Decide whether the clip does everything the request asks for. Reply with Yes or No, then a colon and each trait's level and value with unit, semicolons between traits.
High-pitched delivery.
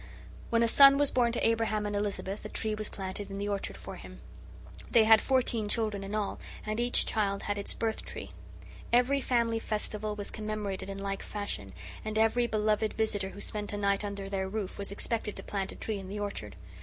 Yes: high, 210 Hz